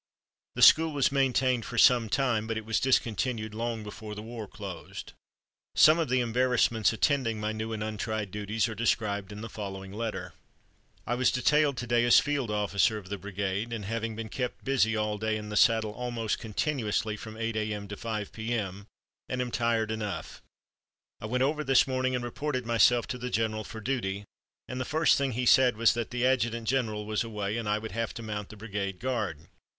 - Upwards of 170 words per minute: Yes, average, 200 wpm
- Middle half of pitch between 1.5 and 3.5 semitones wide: Yes, average, 2.8 semitones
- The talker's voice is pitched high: No, low, 115 Hz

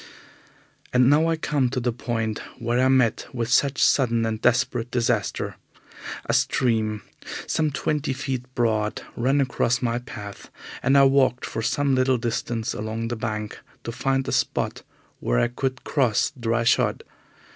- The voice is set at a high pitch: No, low, 120 Hz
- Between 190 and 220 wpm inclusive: No, average, 155 wpm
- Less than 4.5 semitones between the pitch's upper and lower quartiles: Yes, average, 2.7 semitones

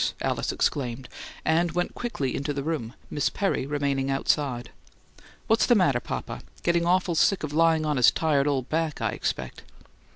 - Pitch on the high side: No, medium, 150 Hz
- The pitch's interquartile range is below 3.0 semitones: No, average, 3.7 semitones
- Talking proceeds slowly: No, average, 165 wpm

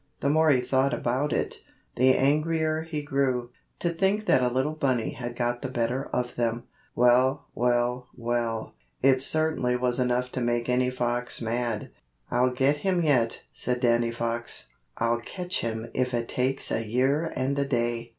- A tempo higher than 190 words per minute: No, average, 170 wpm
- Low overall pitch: Yes, low, 125 Hz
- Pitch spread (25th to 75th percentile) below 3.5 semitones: Yes, narrow, 2.5 semitones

